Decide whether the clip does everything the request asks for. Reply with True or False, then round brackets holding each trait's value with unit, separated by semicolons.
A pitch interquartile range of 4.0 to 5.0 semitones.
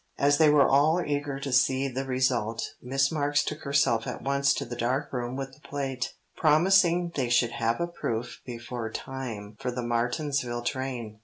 False (3.0 semitones)